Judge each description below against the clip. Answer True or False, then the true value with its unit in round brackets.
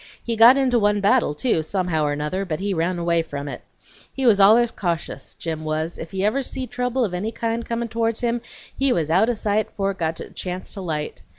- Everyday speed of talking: False (230 wpm)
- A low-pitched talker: False (195 Hz)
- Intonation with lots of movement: True (5.9 semitones)